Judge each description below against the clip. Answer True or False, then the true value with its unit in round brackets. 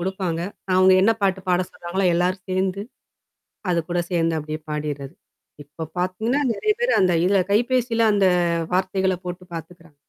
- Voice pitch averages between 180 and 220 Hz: True (185 Hz)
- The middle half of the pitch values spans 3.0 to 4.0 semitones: False (2.4 semitones)